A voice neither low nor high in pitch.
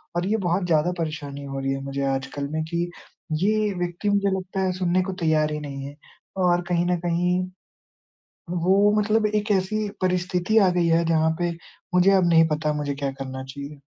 Yes: medium, 175 Hz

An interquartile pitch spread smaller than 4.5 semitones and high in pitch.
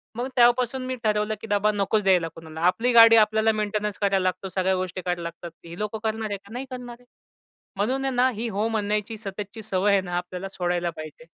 Yes: average, 3.3 semitones; high, 210 Hz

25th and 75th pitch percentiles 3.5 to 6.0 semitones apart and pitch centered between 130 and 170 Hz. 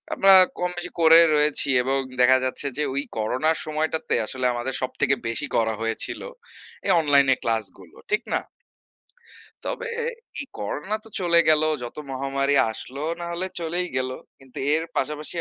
Yes: average, 3.8 semitones; medium, 140 Hz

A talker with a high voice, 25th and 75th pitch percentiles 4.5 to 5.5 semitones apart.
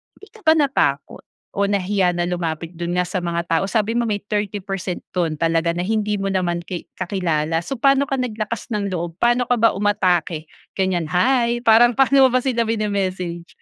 Yes: high, 195 Hz; average, 4.9 semitones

